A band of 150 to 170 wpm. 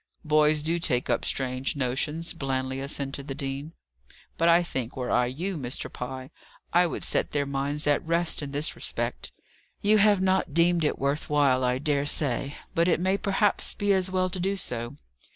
No: average, 190 wpm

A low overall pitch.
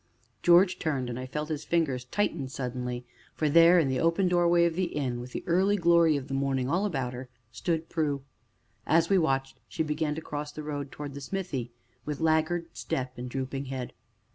No: medium, 150 Hz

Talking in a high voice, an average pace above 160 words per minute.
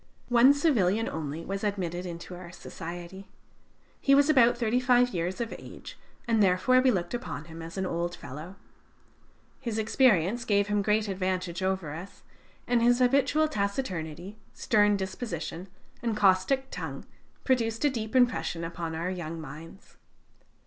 No: high, 195 Hz; average, 150 wpm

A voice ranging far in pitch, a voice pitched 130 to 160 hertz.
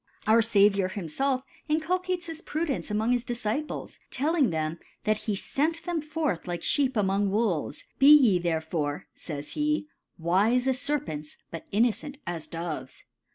No: wide, 9.0 semitones; high, 220 Hz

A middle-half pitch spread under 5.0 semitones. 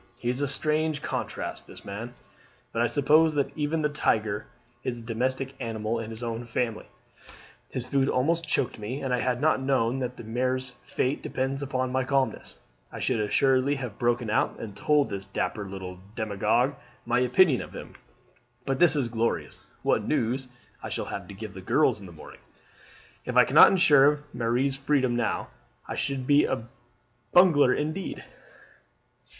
Yes: average, 3.5 semitones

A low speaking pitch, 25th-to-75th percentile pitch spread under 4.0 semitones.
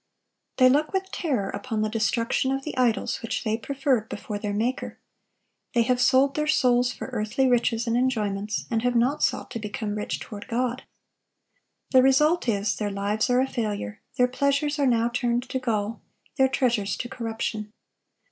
No: high, 240 Hz; average, 3.4 semitones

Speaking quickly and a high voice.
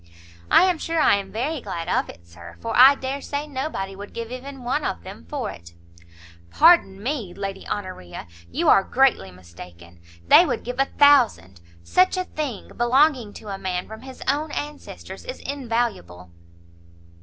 No: average, 170 wpm; high, 235 Hz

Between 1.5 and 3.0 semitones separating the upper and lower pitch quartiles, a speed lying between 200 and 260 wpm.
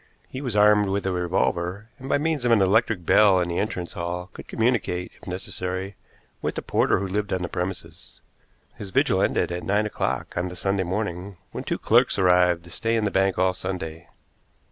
Yes: average, 2.7 semitones; fast, 205 wpm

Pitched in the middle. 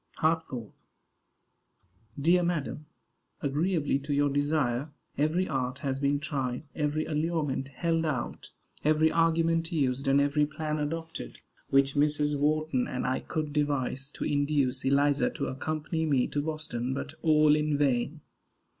Yes: medium, 145 Hz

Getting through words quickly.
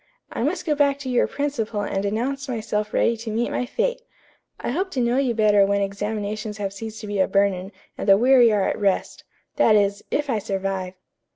Yes: fast, 210 wpm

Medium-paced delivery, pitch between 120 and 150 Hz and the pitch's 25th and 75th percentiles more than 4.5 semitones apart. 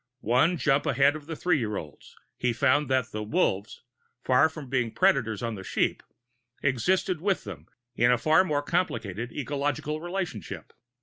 Yes: average, 165 wpm; low, 135 Hz; average, 5.1 semitones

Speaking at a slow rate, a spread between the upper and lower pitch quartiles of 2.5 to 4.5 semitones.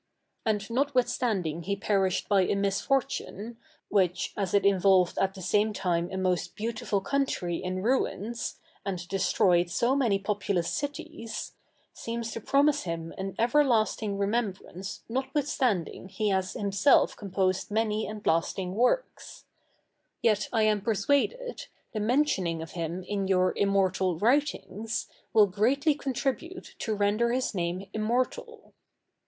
Yes: slow, 130 wpm; average, 4.1 semitones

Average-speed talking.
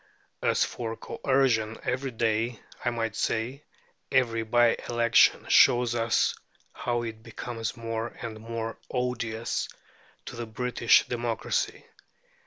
No: slow, 115 wpm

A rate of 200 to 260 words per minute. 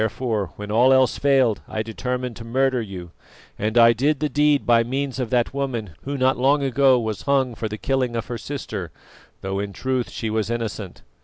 Yes: fast, 205 wpm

